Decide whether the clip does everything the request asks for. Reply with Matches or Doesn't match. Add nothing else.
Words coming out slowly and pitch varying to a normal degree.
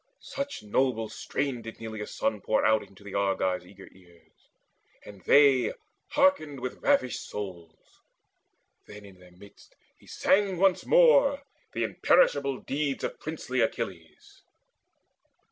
Doesn't match